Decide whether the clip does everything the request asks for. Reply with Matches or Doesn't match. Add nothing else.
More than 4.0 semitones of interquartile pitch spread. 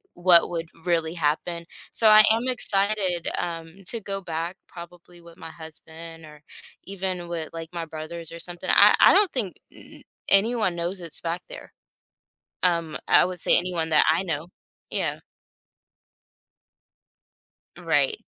Doesn't match